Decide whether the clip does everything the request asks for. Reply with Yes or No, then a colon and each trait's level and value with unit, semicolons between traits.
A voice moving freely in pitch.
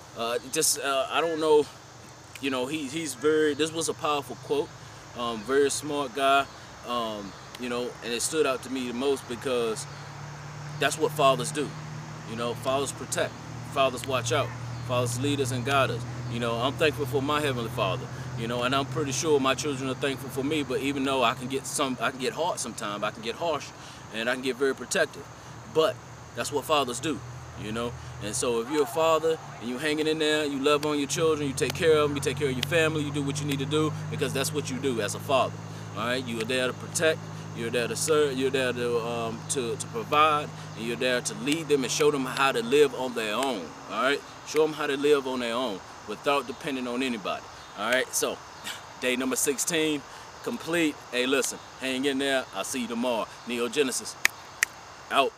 No: average, 3.3 semitones